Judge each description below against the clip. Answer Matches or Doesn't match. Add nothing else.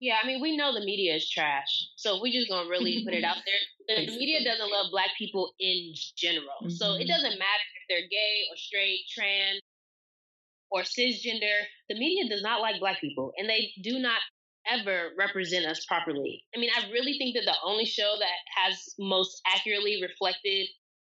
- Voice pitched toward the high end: Matches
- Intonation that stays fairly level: Doesn't match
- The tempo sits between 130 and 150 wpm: Doesn't match